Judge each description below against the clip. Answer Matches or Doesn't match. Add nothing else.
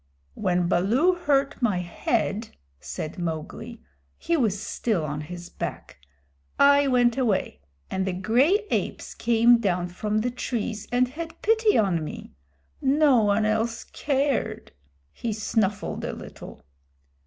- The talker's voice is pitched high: Matches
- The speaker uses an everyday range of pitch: Doesn't match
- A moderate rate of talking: Doesn't match